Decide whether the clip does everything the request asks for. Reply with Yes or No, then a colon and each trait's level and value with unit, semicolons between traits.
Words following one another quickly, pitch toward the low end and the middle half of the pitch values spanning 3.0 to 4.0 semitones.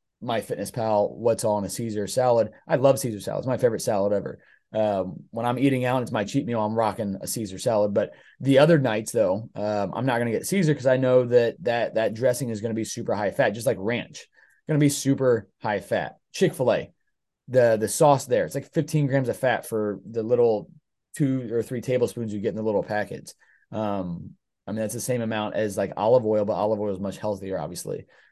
Yes: fast, 220 wpm; low, 115 Hz; average, 3.7 semitones